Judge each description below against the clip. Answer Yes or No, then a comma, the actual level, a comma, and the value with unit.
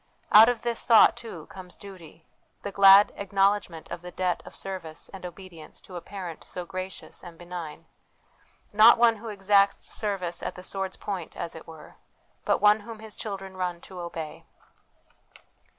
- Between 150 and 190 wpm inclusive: Yes, average, 165 wpm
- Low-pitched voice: No, high, 190 Hz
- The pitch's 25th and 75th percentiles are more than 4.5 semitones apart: No, average, 2.7 semitones